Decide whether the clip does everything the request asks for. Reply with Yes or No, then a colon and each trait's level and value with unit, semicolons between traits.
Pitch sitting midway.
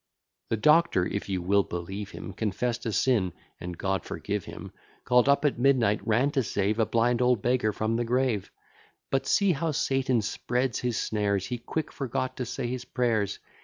No: low, 120 Hz